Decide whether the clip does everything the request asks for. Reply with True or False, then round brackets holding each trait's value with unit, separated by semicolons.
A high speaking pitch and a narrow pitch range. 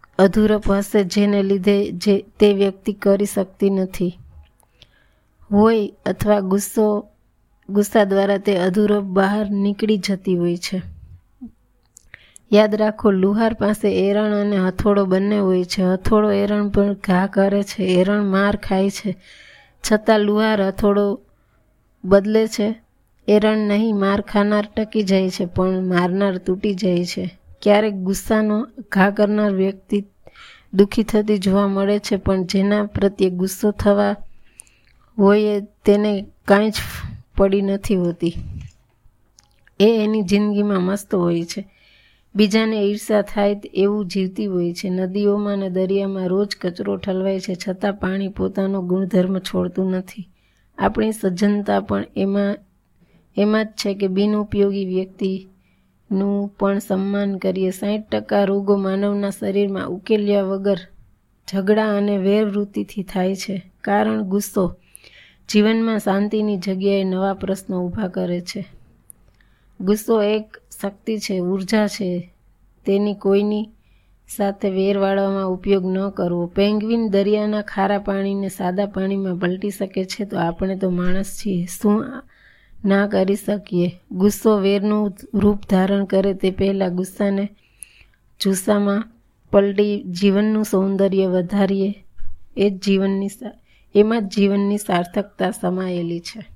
True (200 Hz; 1.5 semitones)